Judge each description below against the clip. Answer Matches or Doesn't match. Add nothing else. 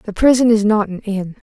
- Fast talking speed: Matches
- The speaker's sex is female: Matches